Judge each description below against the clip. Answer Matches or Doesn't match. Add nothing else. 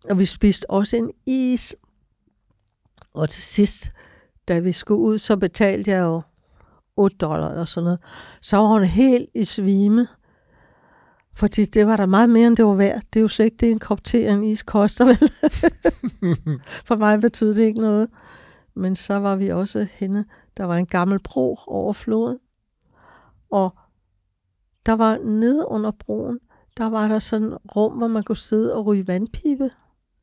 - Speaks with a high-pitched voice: Matches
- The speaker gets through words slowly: Doesn't match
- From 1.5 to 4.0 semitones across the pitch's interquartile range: Matches